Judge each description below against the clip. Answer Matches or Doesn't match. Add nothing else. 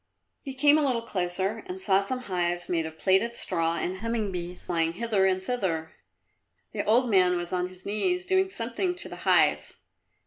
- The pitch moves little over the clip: Doesn't match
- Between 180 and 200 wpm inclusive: Matches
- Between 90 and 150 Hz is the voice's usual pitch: Doesn't match